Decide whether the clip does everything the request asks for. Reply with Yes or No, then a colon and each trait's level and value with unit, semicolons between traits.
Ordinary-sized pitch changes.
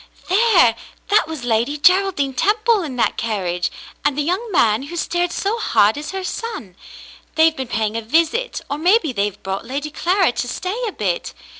No: wide, 8.8 semitones